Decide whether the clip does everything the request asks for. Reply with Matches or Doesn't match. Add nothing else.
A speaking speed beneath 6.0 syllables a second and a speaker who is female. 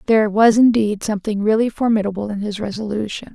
Doesn't match